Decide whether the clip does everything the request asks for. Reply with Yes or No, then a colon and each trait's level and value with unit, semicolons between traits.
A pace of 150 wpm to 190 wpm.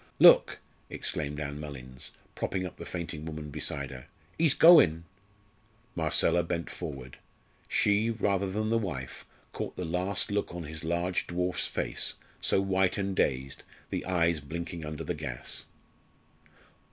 No: average, 140 wpm